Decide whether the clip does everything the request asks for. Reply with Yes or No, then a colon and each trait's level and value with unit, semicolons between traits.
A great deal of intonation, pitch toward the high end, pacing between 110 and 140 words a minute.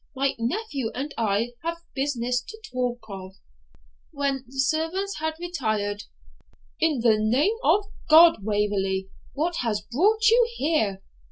Yes: wide, 7.2 semitones; very high, 270 Hz; slow, 135 wpm